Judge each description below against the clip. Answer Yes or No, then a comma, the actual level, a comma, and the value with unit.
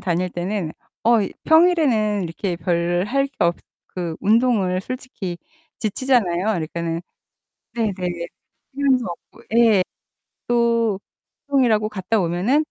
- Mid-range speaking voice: No, high, 210 Hz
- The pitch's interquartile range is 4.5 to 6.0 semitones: Yes, wide, 5.4 semitones